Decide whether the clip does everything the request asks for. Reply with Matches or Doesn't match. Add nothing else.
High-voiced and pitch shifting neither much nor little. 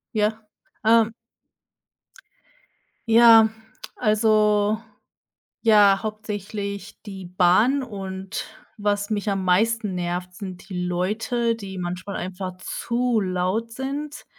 Matches